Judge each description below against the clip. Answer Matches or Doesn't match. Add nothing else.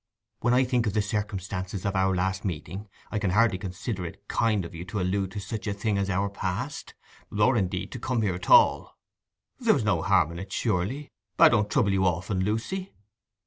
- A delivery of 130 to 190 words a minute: Doesn't match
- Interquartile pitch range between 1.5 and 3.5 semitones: Matches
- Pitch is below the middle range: Matches